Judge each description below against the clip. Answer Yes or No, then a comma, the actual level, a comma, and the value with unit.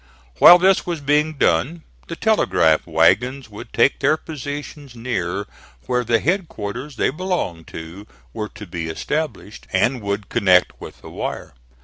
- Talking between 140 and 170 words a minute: Yes, average, 145 wpm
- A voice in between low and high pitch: No, low, 125 Hz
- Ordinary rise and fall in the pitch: No, wide, 7.2 semitones